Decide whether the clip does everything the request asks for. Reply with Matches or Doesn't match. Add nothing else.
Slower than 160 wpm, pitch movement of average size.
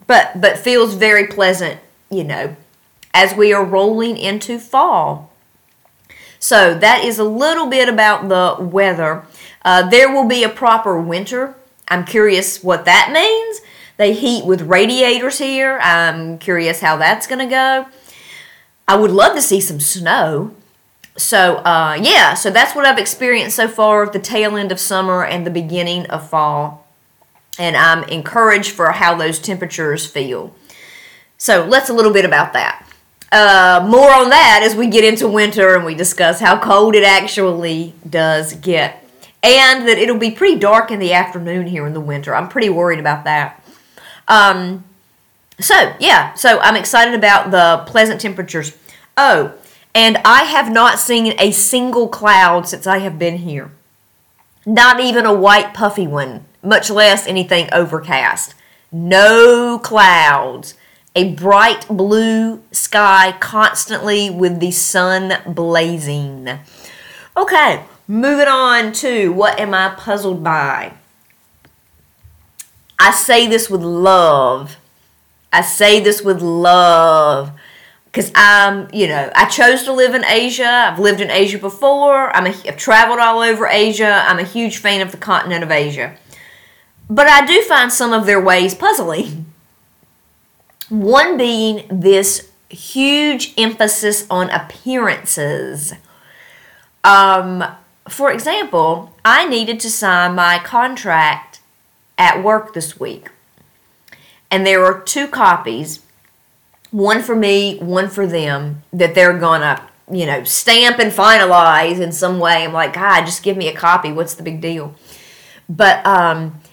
Matches